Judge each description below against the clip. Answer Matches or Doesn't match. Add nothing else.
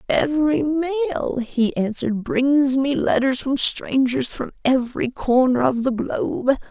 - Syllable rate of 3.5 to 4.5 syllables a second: Matches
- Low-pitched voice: Doesn't match